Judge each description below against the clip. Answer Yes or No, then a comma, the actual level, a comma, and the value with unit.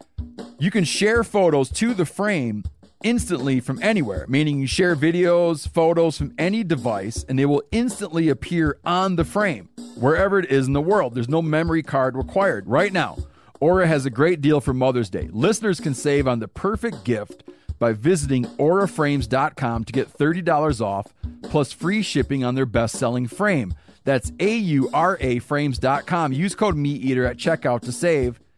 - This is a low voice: No, medium, 145 Hz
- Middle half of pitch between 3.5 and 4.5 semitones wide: No, wide, 5.6 semitones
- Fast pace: No, average, 170 wpm